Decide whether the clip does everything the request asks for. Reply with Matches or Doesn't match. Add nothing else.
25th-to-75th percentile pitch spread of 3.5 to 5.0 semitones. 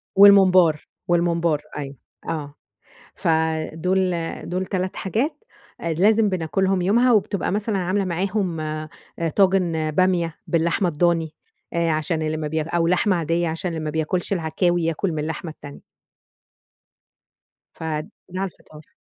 Doesn't match